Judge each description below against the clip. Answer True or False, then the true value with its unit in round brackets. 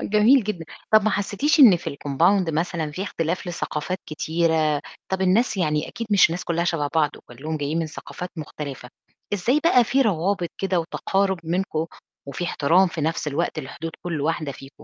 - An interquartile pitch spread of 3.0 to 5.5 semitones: True (3.9 semitones)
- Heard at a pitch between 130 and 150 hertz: False (170 Hz)